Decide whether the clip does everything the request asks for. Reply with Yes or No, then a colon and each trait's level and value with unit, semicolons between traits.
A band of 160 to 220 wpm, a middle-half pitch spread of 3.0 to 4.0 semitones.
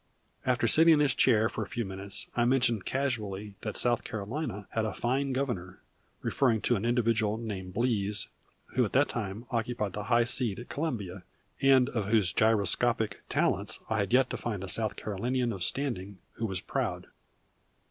Yes: average, 180 wpm; average, 3.4 semitones